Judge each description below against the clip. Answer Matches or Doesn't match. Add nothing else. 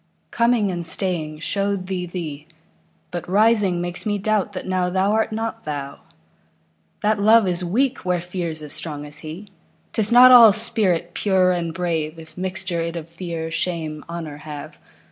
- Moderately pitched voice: Matches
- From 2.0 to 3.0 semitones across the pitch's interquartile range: Doesn't match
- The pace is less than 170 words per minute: Matches